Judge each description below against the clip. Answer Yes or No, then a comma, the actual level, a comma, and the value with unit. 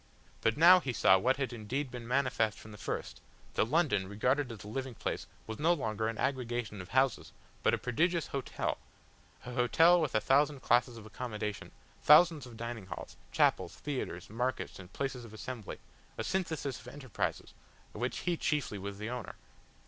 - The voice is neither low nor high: No, low, 125 Hz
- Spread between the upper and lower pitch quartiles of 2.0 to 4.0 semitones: No, average, 4.4 semitones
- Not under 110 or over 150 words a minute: No, average, 180 wpm